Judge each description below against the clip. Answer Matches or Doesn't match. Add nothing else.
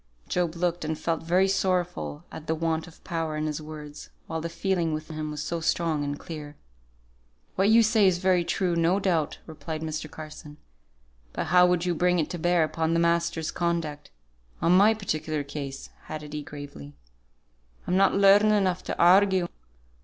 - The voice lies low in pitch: Doesn't match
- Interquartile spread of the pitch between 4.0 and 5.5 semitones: Doesn't match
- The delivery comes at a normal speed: Matches